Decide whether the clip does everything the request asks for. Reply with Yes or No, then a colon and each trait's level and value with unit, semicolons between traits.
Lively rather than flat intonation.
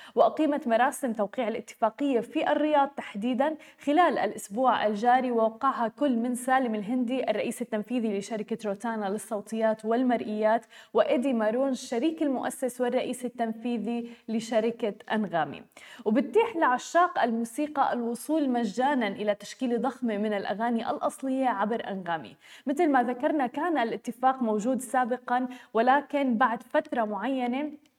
No: average, 3.2 semitones